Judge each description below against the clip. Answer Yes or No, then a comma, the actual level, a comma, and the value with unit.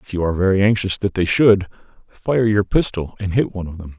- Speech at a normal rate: No, fast, 240 wpm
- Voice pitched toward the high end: No, very low, 95 Hz